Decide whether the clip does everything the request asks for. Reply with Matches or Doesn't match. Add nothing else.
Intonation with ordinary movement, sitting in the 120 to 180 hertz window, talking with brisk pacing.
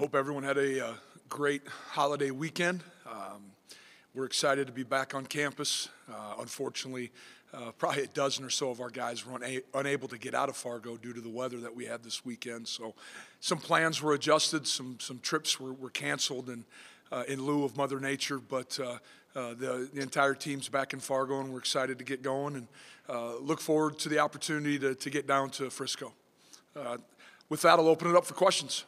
Doesn't match